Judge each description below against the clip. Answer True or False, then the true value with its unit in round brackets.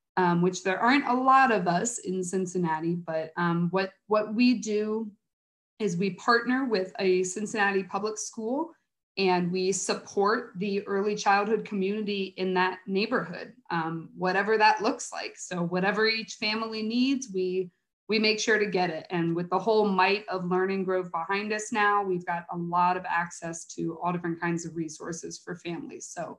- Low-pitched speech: False (195 Hz)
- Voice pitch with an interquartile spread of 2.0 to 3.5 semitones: True (3.1 semitones)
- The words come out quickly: False (175 wpm)